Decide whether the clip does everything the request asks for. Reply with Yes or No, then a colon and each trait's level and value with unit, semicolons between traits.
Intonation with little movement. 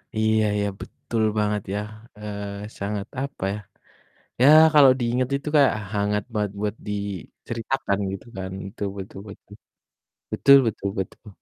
Yes: narrow, 2.2 semitones